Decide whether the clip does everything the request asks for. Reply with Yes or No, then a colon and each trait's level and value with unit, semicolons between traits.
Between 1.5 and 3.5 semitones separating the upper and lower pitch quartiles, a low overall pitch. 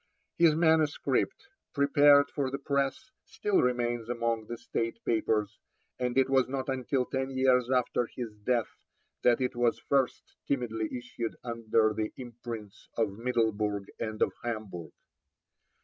Yes: average, 3.0 semitones; low, 120 Hz